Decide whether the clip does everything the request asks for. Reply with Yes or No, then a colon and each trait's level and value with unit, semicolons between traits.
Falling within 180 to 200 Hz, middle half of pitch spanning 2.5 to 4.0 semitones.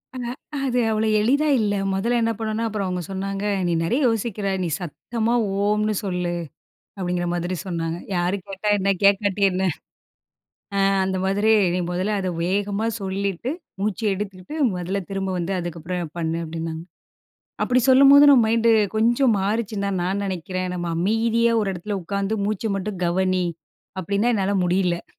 Yes: high, 195 Hz; average, 3.2 semitones